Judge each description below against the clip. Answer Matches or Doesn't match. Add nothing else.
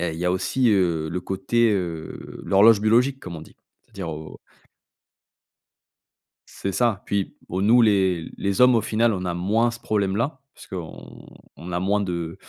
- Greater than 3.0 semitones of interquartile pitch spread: Matches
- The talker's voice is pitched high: Doesn't match